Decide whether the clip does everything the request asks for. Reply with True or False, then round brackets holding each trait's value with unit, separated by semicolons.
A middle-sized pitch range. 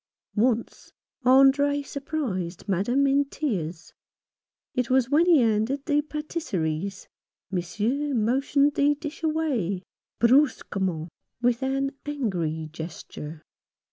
False (7.1 semitones)